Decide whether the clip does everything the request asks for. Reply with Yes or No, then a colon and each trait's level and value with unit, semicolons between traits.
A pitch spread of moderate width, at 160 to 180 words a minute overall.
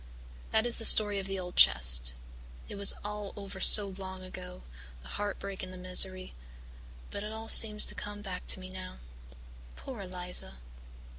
No: narrow, 2.1 semitones; average, 170 wpm